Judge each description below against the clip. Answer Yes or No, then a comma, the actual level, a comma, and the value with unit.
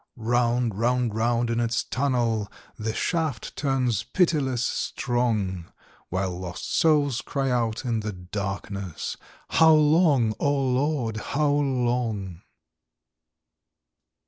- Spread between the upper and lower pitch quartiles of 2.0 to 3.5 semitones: No, average, 4.0 semitones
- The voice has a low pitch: Yes, low, 120 Hz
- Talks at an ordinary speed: No, slow, 105 wpm